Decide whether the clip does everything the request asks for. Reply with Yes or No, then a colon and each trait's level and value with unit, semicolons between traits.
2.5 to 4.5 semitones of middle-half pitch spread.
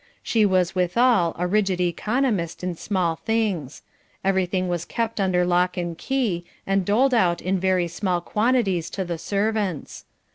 Yes: average, 3.4 semitones